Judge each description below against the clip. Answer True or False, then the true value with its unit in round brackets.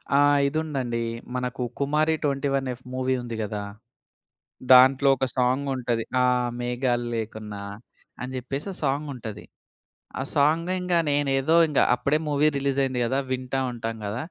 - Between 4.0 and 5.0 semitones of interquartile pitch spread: False (2.6 semitones)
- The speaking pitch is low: True (130 Hz)